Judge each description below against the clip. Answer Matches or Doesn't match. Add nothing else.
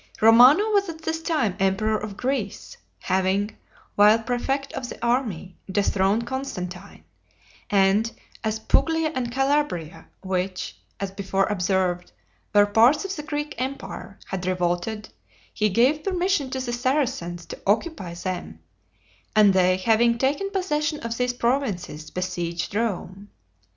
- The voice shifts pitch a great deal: Matches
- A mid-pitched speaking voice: Doesn't match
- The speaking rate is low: Matches